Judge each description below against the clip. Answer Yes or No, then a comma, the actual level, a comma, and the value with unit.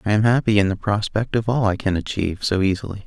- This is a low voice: Yes, low, 105 Hz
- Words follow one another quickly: Yes, fast, 255 wpm